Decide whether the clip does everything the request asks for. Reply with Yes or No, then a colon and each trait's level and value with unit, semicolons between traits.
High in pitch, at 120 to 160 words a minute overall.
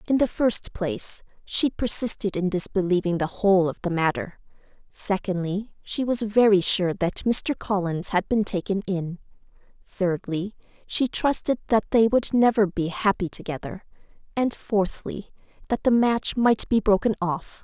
Yes: high, 200 Hz; average, 150 wpm